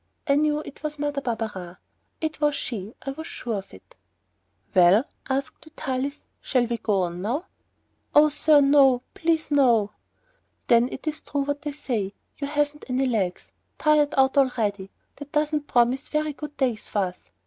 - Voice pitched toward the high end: Yes, very high, 270 Hz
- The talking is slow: No, average, 170 wpm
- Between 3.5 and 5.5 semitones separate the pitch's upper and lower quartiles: Yes, average, 4.7 semitones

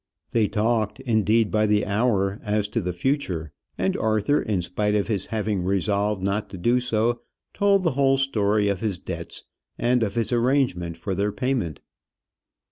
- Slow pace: No, average, 170 wpm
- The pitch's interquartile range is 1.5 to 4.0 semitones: Yes, average, 3.3 semitones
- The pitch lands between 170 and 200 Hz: No, low, 105 Hz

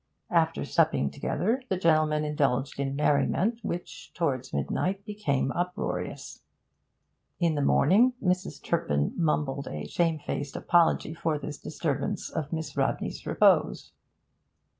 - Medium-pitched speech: Yes, medium, 155 Hz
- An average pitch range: Yes, average, 4.0 semitones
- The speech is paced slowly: Yes, slow, 120 wpm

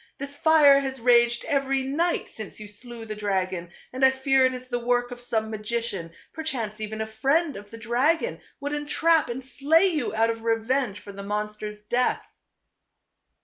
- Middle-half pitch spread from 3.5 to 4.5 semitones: Yes, average, 4.2 semitones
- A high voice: Yes, high, 245 Hz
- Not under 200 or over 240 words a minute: No, average, 185 wpm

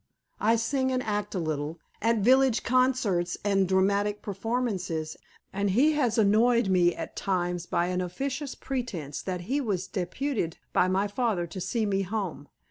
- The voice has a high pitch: Yes, high, 200 Hz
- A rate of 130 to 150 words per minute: No, average, 160 wpm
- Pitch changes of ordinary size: Yes, average, 4.9 semitones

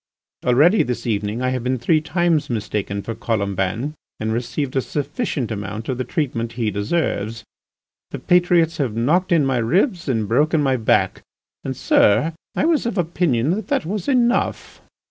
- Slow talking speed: No, average, 165 wpm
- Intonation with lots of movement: Yes, wide, 7.0 semitones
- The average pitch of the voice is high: No, low, 130 Hz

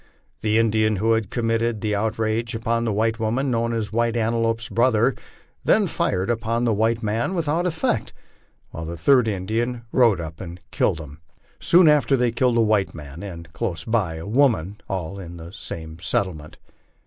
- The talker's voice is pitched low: Yes, low, 110 Hz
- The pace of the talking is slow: No, average, 175 wpm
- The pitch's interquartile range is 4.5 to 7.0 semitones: No, average, 3.8 semitones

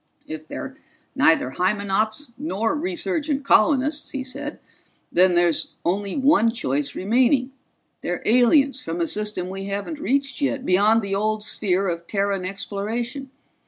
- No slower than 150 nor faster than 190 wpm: No, slow, 135 wpm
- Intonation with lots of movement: Yes, wide, 6.1 semitones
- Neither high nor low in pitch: No, high, 215 Hz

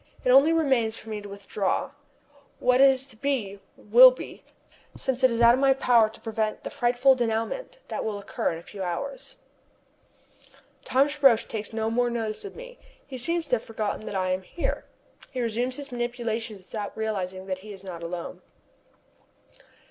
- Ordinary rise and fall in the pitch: Yes, average, 4.1 semitones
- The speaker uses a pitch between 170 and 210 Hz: No, high, 230 Hz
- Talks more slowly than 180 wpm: No, average, 185 wpm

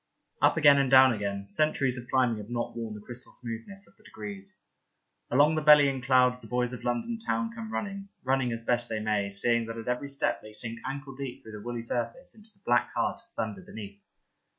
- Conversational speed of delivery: No, fast, 220 wpm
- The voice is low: Yes, low, 120 Hz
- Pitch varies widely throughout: No, average, 3.6 semitones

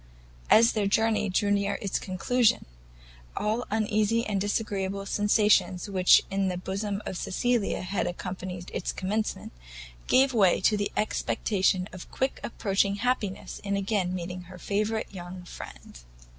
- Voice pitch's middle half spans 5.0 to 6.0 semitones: No, narrow, 2.4 semitones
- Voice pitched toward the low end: No, high, 200 Hz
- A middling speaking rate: Yes, average, 145 wpm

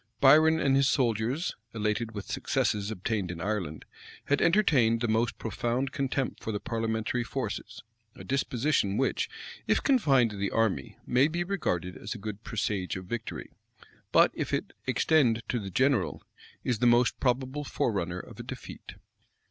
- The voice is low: Yes, low, 115 Hz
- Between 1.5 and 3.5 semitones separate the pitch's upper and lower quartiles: No, average, 4.3 semitones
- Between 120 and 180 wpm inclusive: Yes, average, 160 wpm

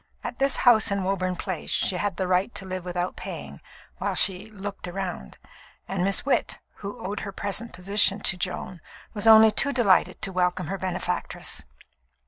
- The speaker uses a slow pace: No, average, 175 wpm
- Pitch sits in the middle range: No, high, 195 Hz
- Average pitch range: No, narrow, 2.1 semitones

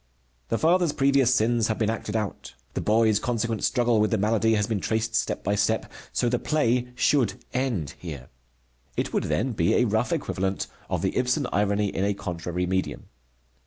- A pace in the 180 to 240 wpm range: Yes, average, 185 wpm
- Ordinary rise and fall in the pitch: Yes, average, 3.3 semitones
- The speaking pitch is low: Yes, low, 110 Hz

